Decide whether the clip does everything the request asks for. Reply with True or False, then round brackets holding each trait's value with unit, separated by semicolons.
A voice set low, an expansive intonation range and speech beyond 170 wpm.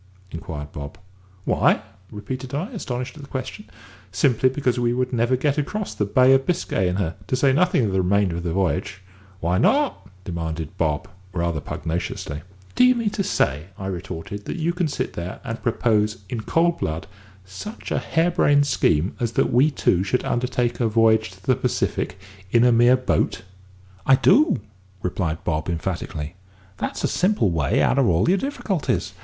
True (115 Hz; 7.3 semitones; 180 wpm)